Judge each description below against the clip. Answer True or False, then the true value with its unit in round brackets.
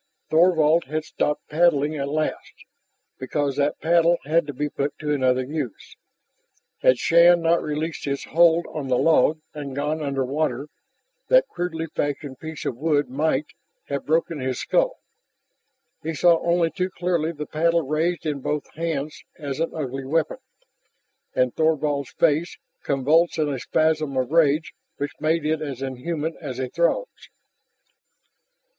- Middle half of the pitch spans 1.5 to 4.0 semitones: True (2.8 semitones)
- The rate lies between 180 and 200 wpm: False (150 wpm)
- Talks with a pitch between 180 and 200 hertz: False (155 Hz)